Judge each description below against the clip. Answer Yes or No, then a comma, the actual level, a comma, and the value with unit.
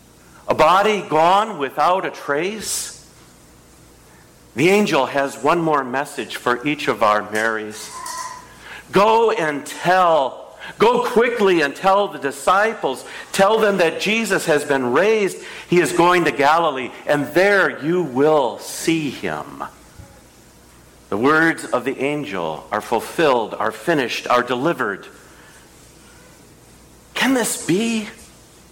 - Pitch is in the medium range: Yes, medium, 160 Hz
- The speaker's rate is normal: No, slow, 120 wpm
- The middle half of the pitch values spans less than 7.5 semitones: No, wide, 8.0 semitones